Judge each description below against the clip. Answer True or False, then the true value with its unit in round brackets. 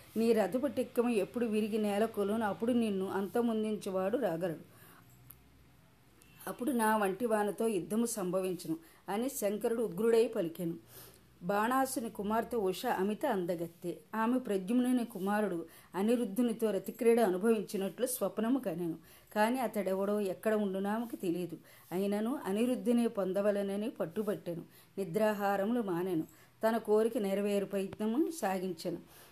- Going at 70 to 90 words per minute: False (100 wpm)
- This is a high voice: True (210 Hz)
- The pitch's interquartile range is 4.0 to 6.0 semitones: False (3.3 semitones)